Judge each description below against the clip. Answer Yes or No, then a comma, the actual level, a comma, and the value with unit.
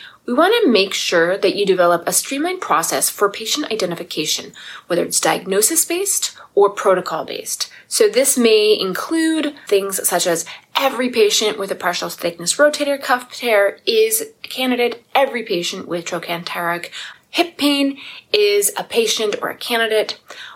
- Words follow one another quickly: No, average, 150 wpm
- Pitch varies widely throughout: Yes, wide, 8.1 semitones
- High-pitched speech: Yes, high, 230 Hz